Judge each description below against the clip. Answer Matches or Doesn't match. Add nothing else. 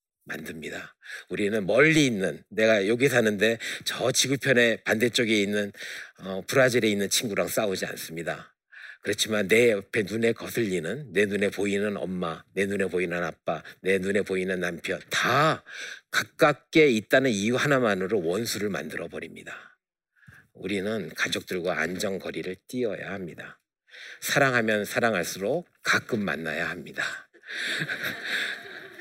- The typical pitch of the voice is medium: Doesn't match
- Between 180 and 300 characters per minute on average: Matches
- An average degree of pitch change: Matches